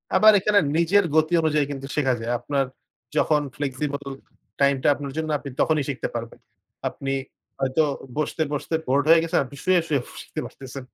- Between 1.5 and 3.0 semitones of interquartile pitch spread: Yes, average, 2.7 semitones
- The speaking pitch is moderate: Yes, medium, 145 Hz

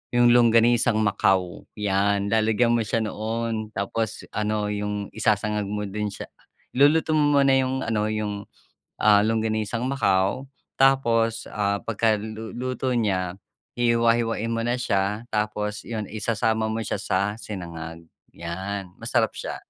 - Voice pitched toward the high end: No, low, 110 Hz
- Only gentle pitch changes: Yes, narrow, 2.2 semitones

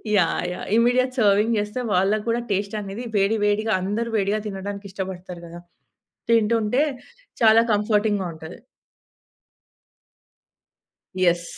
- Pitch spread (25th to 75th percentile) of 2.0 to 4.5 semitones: Yes, narrow, 2.5 semitones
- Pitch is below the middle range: No, high, 205 Hz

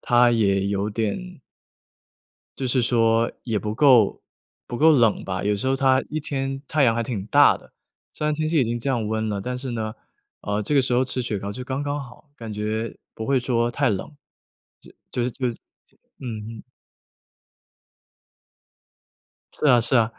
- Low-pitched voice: Yes, low, 120 Hz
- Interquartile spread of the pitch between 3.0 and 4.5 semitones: Yes, average, 3.5 semitones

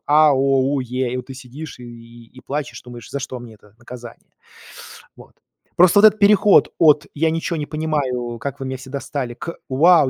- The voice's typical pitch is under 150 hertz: Yes, low, 135 Hz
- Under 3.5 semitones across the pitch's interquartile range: No, average, 4.0 semitones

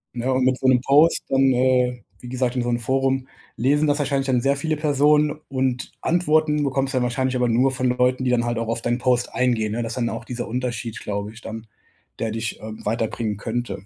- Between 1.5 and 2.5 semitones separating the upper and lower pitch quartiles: Yes, narrow, 2.2 semitones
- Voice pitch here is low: Yes, low, 125 Hz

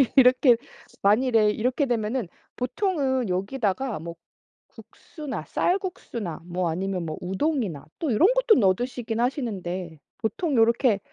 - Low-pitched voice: No, high, 230 Hz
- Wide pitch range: Yes, wide, 5.7 semitones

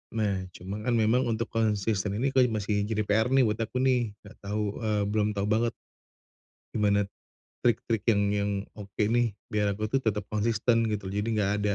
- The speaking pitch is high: No, low, 105 Hz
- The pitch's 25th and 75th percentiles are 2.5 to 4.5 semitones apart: No, narrow, 1.9 semitones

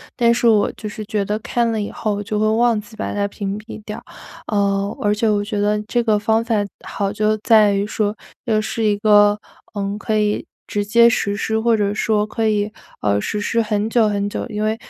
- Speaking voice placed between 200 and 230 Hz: Yes, high, 210 Hz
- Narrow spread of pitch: Yes, narrow, 1.2 semitones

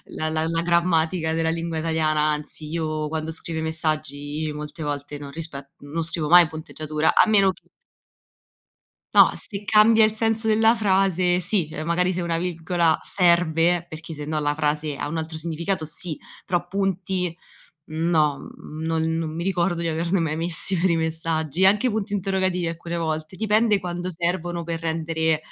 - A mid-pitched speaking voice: Yes, medium, 165 Hz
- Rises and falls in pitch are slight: Yes, narrow, 2.3 semitones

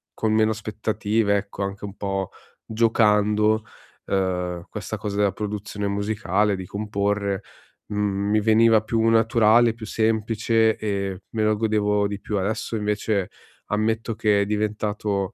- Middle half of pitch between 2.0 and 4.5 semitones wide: No, narrow, 1.4 semitones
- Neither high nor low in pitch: No, low, 105 Hz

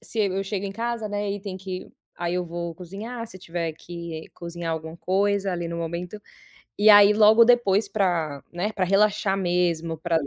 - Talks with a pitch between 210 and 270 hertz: No, medium, 185 Hz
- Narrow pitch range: No, average, 3.2 semitones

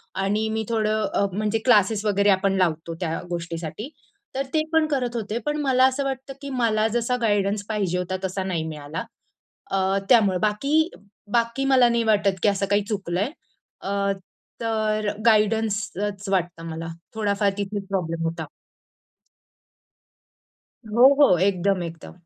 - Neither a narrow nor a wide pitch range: Yes, average, 3.3 semitones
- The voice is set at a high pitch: Yes, high, 205 Hz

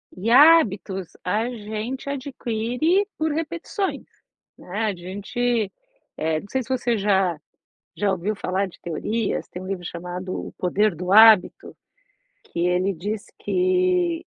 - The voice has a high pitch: Yes, high, 215 Hz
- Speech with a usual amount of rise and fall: No, wide, 5.9 semitones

